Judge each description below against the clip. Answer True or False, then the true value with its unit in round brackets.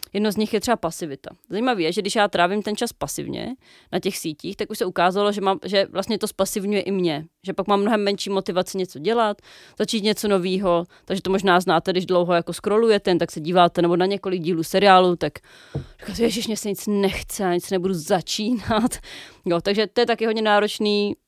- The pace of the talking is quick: True (215 wpm)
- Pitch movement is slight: False (3.0 semitones)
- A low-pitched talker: False (195 Hz)